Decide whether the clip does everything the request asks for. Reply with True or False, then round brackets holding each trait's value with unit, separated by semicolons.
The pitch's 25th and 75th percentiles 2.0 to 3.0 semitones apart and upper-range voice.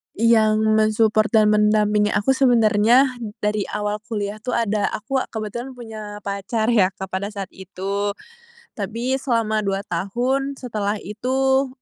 True (2.4 semitones; 215 Hz)